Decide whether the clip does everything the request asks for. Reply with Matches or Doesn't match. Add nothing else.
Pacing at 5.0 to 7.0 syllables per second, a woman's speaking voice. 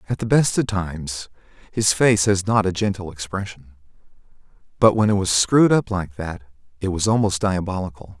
Doesn't match